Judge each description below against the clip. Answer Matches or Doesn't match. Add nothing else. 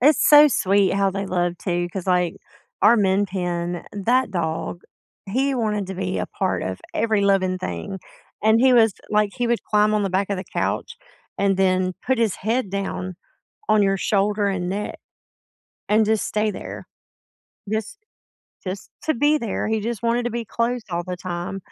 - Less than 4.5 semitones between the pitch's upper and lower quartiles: Matches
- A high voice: Matches